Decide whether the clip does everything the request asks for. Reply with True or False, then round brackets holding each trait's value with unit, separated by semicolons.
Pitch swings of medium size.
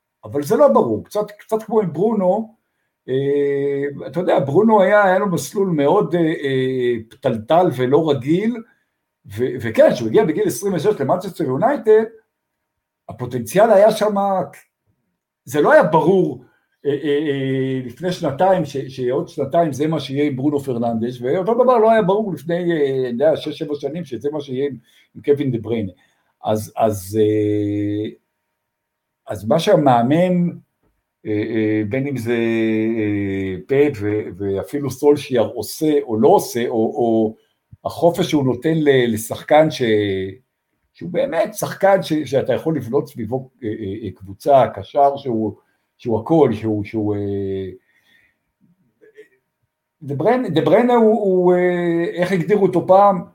False (7.6 semitones)